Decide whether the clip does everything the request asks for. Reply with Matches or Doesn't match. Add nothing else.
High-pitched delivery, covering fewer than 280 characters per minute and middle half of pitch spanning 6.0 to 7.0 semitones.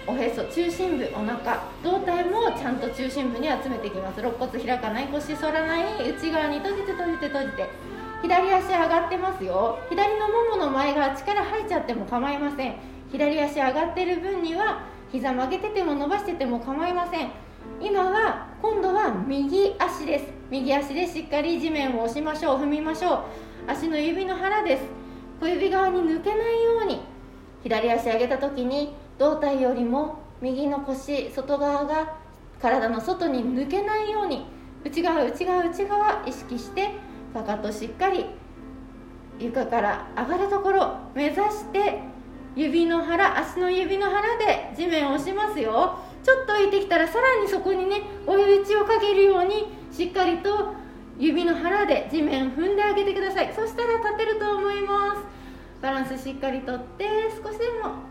Doesn't match